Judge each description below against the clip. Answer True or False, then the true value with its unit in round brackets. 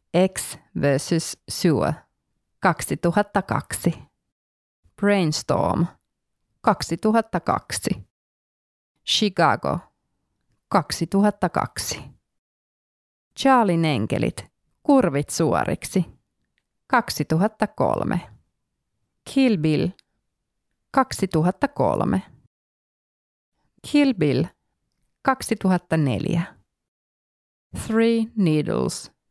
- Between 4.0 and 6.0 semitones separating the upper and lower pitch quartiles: True (5.5 semitones)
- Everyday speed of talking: False (45 wpm)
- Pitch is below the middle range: False (180 Hz)